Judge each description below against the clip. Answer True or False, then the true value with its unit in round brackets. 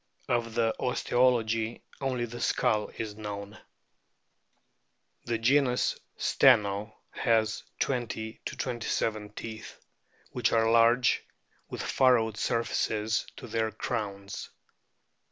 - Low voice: True (115 Hz)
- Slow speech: True (95 wpm)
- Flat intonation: True (1.8 semitones)